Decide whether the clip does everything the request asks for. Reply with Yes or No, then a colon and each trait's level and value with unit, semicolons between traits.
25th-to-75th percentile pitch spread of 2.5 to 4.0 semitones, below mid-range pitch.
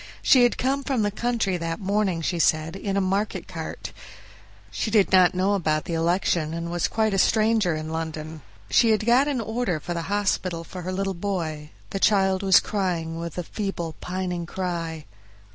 No: average, 3.7 semitones; medium, 185 Hz